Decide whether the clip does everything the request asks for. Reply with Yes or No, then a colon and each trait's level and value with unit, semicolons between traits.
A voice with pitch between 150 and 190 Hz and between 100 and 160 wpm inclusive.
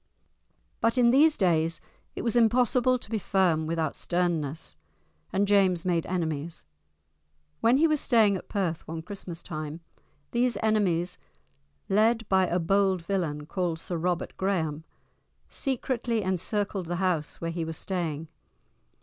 Yes: medium, 185 Hz; average, 140 wpm